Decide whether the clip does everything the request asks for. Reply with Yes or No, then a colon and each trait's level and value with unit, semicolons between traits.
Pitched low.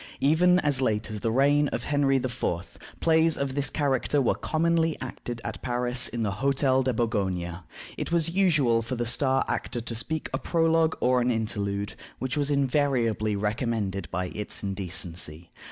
Yes: low, 125 Hz